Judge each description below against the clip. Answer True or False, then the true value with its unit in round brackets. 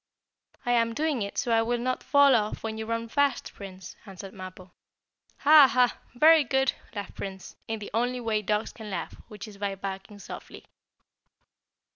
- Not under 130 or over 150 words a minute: False (175 wpm)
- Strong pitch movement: False (3.8 semitones)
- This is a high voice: True (225 Hz)